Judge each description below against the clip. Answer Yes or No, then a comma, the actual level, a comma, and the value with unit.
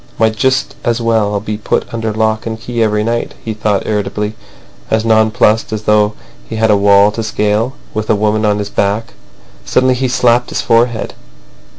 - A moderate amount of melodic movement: No, narrow, 1.5 semitones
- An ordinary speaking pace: Yes, average, 185 wpm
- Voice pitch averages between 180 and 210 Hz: No, low, 110 Hz